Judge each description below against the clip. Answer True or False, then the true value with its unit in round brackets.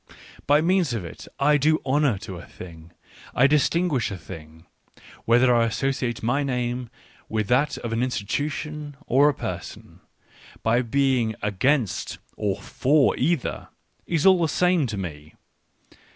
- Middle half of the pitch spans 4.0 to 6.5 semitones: True (5.2 semitones)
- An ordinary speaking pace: True (150 wpm)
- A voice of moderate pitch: False (125 Hz)